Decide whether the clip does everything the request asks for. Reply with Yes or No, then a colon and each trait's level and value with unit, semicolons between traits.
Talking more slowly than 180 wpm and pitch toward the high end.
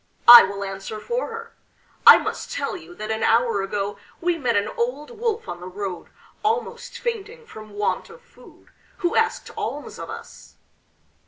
Yes: average, 170 wpm; high, 245 Hz